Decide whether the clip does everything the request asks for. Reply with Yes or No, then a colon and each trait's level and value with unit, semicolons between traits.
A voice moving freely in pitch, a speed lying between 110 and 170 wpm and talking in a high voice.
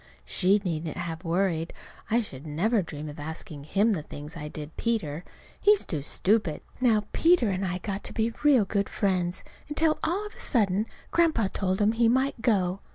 No: wide, 5.8 semitones; average, 185 wpm; high, 195 Hz